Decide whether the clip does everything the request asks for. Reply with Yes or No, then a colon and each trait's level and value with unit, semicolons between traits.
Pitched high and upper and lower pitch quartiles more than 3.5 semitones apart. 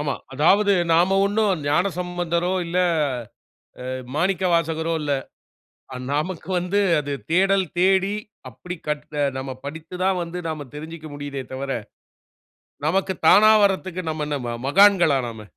No: medium, 170 Hz; average, 4.2 semitones